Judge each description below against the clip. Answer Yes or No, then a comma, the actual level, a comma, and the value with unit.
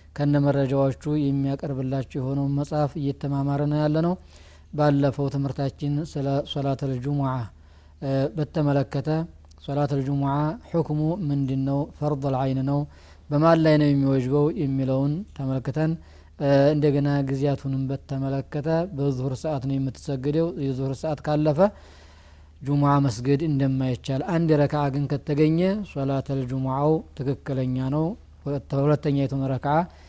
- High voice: No, medium, 140 Hz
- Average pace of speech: Yes, average, 100 wpm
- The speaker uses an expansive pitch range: No, narrow, 1.8 semitones